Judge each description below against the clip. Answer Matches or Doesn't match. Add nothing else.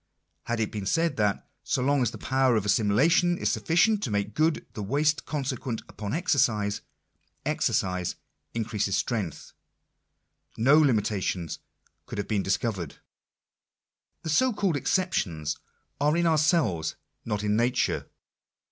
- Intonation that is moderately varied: Doesn't match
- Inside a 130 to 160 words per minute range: Matches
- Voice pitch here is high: Doesn't match